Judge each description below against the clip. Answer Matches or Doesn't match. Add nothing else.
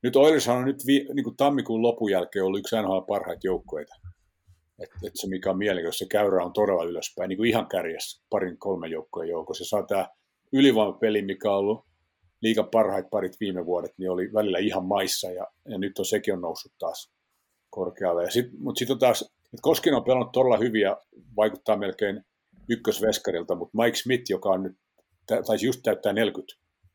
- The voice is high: Doesn't match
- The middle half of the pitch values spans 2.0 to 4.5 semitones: Doesn't match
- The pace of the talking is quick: Matches